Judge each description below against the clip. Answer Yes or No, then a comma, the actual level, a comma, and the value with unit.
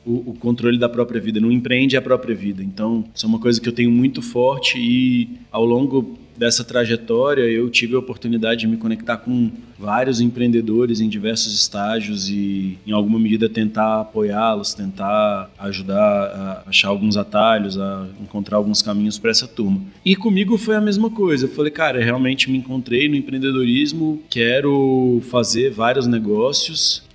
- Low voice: Yes, low, 115 Hz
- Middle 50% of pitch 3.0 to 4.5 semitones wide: Yes, average, 3.3 semitones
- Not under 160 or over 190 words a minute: Yes, average, 170 wpm